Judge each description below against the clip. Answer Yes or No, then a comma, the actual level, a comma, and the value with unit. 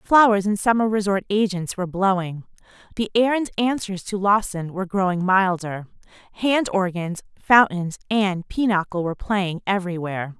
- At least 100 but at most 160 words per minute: Yes, average, 140 wpm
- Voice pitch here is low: No, high, 195 Hz